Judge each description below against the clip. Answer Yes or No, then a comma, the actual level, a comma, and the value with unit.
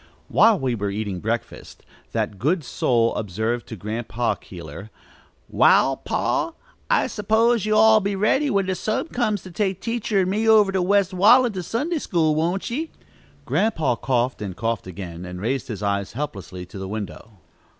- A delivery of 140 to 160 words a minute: No, average, 170 wpm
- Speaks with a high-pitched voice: No, medium, 150 Hz